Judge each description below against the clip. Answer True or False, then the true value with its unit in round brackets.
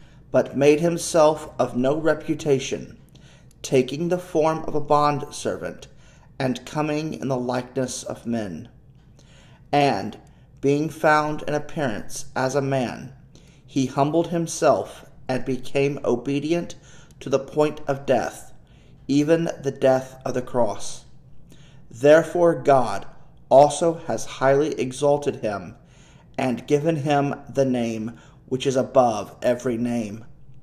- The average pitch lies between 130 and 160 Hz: True (140 Hz)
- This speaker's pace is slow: True (120 wpm)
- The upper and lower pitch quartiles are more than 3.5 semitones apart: False (2.6 semitones)